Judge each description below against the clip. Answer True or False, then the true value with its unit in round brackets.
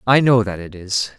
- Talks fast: True (250 wpm)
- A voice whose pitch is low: True (110 Hz)